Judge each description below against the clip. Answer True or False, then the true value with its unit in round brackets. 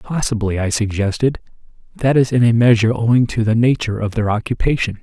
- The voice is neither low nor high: False (115 Hz)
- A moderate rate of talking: True (180 wpm)